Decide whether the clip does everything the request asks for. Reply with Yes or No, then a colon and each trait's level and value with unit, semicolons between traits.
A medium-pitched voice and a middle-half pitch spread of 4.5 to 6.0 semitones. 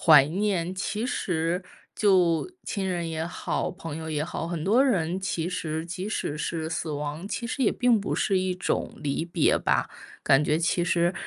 No: medium, 175 Hz; average, 3.1 semitones